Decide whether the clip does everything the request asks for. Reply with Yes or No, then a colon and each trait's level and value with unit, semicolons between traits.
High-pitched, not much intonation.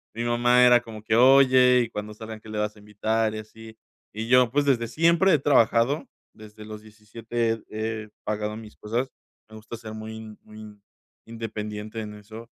No: low, 110 Hz; narrow, 1.8 semitones